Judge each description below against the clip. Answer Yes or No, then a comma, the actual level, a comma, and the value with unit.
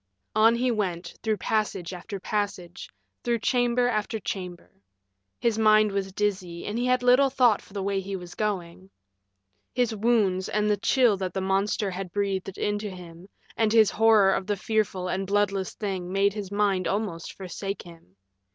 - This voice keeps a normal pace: Yes, average, 170 wpm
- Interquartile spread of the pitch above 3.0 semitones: No, narrow, 2.5 semitones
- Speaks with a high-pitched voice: Yes, high, 200 Hz